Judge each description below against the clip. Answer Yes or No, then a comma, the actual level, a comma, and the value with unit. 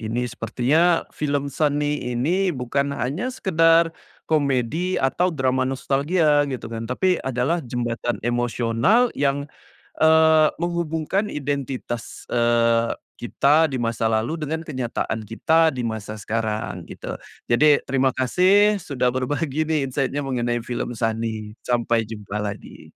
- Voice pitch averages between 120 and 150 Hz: Yes, low, 135 Hz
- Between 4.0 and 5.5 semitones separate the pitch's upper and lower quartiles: Yes, average, 5.0 semitones